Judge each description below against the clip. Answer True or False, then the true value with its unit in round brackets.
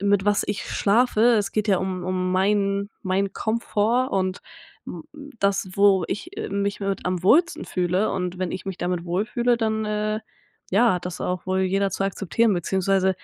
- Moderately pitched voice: False (195 Hz)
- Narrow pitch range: True (2.2 semitones)